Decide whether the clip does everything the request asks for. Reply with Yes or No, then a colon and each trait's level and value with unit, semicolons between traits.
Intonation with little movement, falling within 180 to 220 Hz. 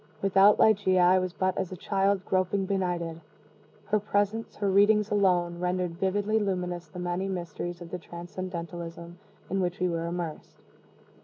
Yes: narrow, 2.0 semitones; medium, 185 Hz